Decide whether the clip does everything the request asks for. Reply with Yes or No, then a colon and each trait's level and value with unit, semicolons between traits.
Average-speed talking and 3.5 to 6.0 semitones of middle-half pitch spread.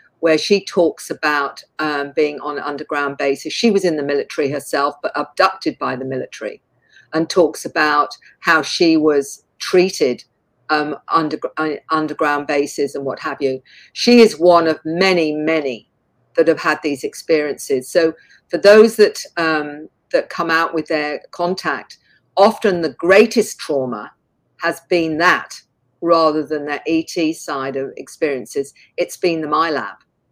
No: average, 150 wpm; average, 3.0 semitones